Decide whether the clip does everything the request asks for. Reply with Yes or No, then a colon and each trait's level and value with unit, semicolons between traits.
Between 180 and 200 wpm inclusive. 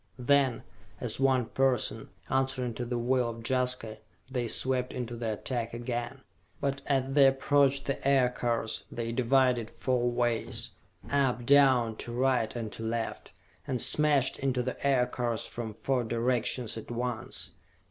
No: average, 145 wpm